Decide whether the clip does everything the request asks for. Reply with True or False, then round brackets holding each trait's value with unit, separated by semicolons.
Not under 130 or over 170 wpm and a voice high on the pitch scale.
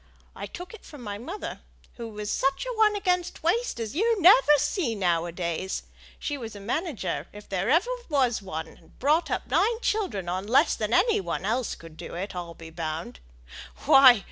False (195 wpm; 235 Hz)